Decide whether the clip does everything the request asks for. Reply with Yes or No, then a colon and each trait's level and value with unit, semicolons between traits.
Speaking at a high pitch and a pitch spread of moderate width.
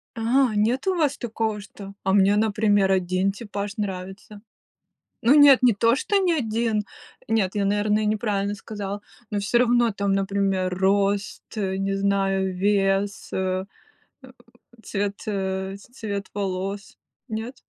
No: high, 205 Hz; narrow, 2.2 semitones